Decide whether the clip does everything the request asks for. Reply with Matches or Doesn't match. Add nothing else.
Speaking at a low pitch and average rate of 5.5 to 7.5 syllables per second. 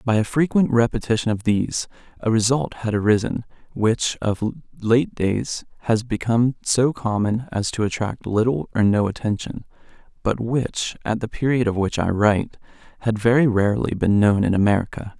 Doesn't match